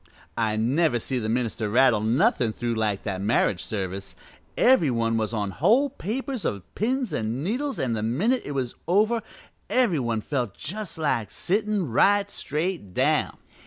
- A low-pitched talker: Yes, low, 130 Hz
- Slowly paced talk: No, average, 160 wpm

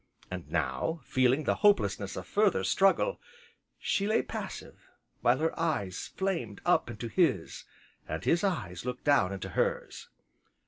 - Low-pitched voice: Yes, low, 130 Hz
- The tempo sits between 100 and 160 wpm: Yes, average, 140 wpm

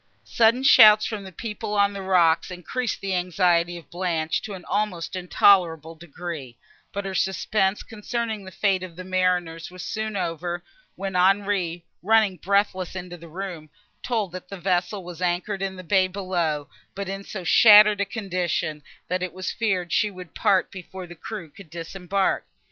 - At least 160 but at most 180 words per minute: Yes, average, 170 wpm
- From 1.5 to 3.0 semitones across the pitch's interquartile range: Yes, narrow, 2.5 semitones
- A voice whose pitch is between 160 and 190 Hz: Yes, medium, 185 Hz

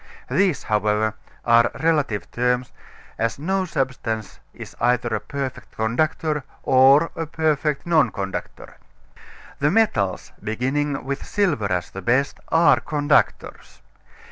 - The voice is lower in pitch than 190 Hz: Yes, low, 135 Hz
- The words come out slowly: Yes, slow, 115 wpm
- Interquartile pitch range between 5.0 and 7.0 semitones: Yes, average, 5.3 semitones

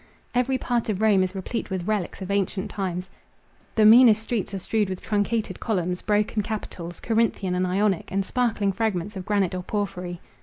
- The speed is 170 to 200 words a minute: Yes, average, 175 wpm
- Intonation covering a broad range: No, average, 2.9 semitones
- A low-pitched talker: No, high, 200 Hz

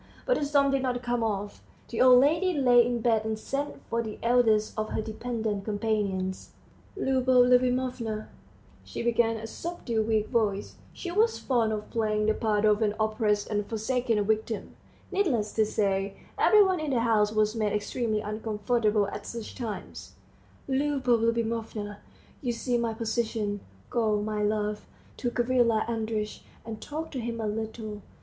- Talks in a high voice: Yes, high, 225 Hz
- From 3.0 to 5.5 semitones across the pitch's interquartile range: No, narrow, 2.6 semitones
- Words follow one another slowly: No, average, 165 wpm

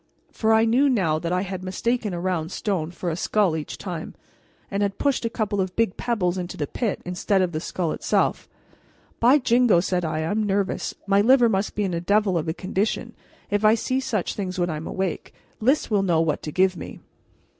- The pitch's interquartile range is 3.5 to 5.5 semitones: Yes, average, 3.8 semitones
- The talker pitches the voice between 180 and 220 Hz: Yes, high, 190 Hz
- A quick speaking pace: Yes, fast, 215 wpm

